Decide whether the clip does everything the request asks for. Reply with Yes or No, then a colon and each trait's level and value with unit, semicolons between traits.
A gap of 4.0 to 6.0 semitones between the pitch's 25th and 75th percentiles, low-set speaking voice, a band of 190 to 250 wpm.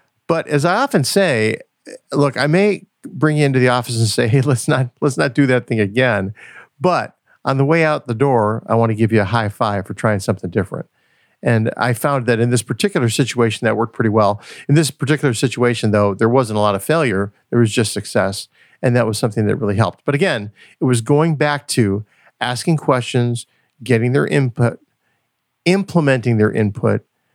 Yes: average, 4.3 semitones; low, 120 Hz; average, 200 wpm